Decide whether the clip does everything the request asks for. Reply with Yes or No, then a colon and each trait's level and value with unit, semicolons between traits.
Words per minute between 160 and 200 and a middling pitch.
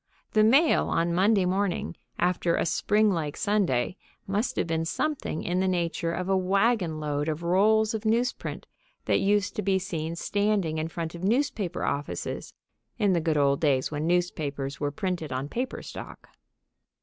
Yes: average, 170 wpm; medium, 180 Hz